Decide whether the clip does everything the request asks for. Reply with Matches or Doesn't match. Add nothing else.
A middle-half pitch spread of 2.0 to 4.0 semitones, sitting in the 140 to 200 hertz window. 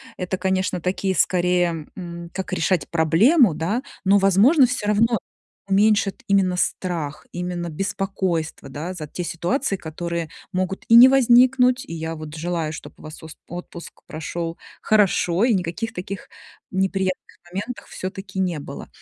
Matches